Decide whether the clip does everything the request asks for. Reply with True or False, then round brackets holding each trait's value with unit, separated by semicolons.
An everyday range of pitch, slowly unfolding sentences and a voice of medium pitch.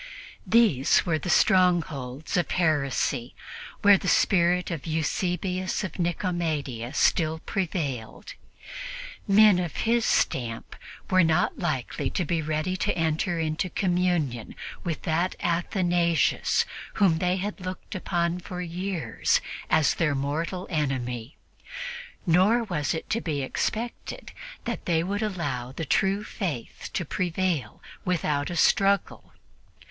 True (3.6 semitones; 120 wpm; 170 Hz)